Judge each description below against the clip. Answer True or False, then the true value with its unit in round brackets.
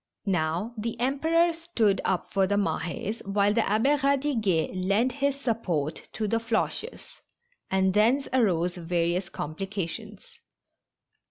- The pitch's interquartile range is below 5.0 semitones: False (5.3 semitones)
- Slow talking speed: True (120 wpm)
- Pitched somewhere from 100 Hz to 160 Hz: False (210 Hz)